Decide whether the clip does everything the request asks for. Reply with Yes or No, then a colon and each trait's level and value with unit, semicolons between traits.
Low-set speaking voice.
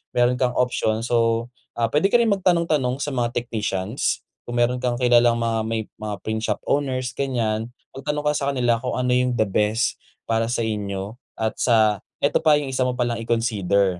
Yes: low, 120 Hz